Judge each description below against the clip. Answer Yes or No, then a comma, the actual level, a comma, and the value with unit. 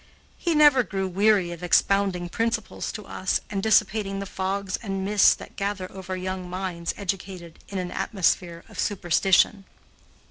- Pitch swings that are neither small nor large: No, narrow, 1.9 semitones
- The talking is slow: No, average, 150 wpm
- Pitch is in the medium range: No, high, 195 Hz